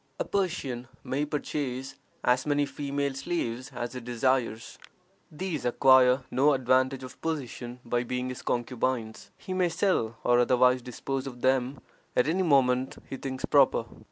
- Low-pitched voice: Yes, low, 130 Hz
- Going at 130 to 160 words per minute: Yes, average, 150 wpm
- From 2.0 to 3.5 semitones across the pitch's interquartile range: Yes, narrow, 2.4 semitones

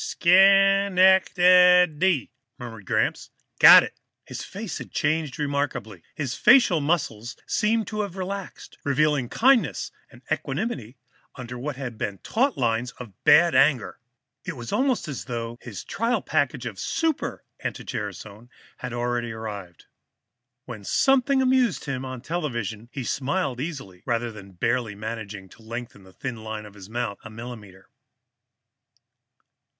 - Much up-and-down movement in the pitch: Yes, wide, 8.1 semitones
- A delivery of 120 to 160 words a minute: Yes, average, 145 wpm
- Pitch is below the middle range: Yes, low, 125 Hz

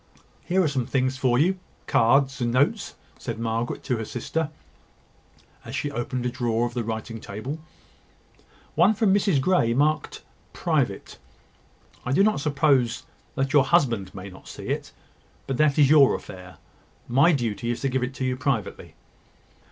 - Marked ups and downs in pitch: No, average, 4.0 semitones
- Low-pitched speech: Yes, low, 130 Hz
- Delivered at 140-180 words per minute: Yes, average, 160 wpm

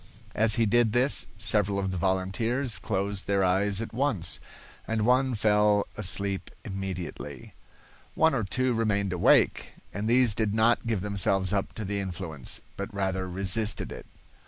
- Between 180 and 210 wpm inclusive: No, average, 155 wpm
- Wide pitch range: No, average, 2.9 semitones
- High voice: No, low, 100 Hz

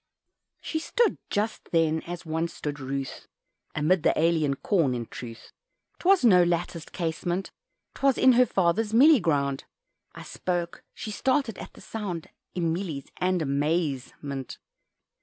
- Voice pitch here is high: No, medium, 170 Hz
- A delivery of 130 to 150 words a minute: Yes, average, 140 wpm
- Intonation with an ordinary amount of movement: No, wide, 5.7 semitones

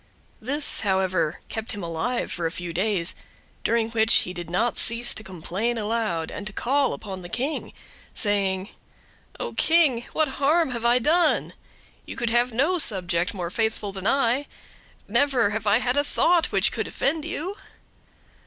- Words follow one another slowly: No, average, 160 wpm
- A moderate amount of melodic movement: No, wide, 6.0 semitones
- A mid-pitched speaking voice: No, high, 225 Hz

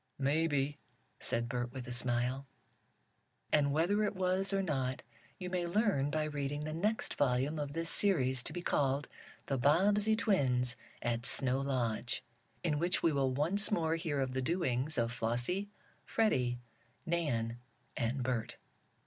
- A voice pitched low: No, medium, 145 Hz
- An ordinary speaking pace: Yes, average, 150 wpm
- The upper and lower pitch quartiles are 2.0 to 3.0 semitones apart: No, average, 5.3 semitones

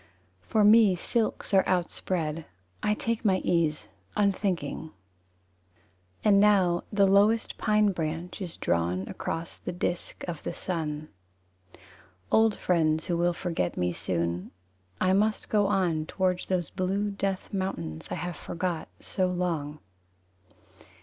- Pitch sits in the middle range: Yes, medium, 180 Hz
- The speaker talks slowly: Yes, slow, 130 wpm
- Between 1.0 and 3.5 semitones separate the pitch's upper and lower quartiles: No, average, 4.3 semitones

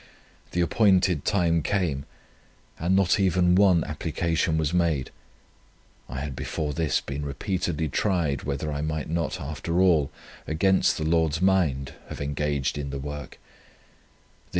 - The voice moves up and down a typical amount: Yes, average, 3.5 semitones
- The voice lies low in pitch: Yes, very low, 80 Hz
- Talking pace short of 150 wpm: Yes, slow, 135 wpm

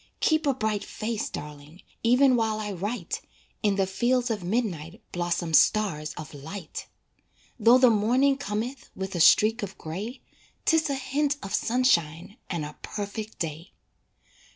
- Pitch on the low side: No, high, 210 Hz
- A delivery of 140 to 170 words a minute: Yes, average, 150 wpm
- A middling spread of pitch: No, wide, 6.0 semitones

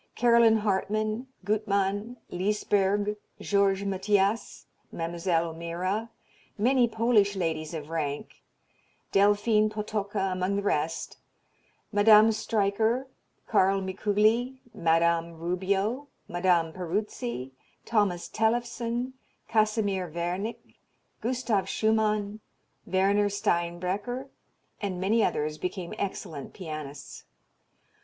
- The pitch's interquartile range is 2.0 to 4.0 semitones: Yes, average, 3.5 semitones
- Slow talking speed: Yes, slow, 85 wpm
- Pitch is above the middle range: Yes, high, 200 Hz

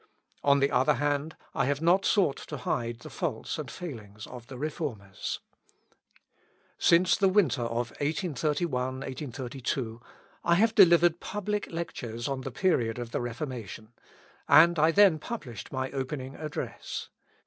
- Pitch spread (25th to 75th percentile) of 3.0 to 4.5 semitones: No, wide, 5.6 semitones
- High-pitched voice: No, medium, 140 Hz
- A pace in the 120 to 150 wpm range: Yes, average, 140 wpm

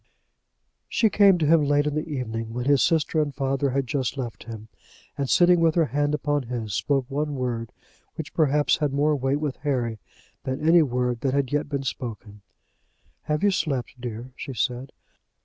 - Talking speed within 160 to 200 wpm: Yes, average, 185 wpm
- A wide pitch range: No, average, 3.3 semitones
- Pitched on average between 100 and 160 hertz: Yes, medium, 140 Hz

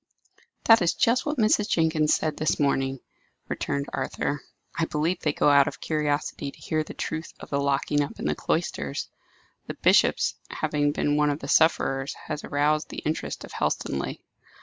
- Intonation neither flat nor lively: No, narrow, 2.0 semitones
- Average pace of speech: Yes, average, 175 wpm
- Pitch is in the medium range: Yes, medium, 150 Hz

